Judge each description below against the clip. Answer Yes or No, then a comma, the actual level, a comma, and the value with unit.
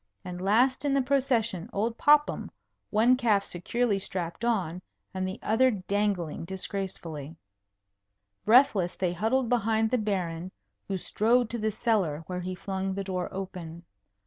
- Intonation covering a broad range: No, average, 4.4 semitones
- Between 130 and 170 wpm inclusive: Yes, average, 145 wpm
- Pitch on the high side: Yes, high, 200 Hz